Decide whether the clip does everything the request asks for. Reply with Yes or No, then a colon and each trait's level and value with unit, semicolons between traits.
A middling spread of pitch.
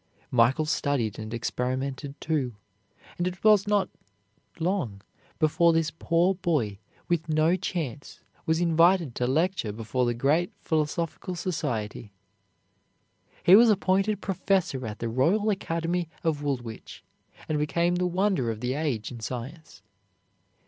No: wide, 6.0 semitones